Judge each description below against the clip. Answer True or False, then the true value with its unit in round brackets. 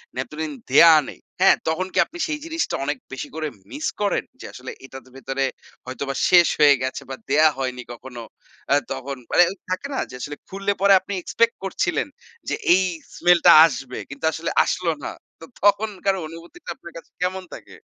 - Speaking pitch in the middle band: True (160 Hz)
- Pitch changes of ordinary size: False (6.1 semitones)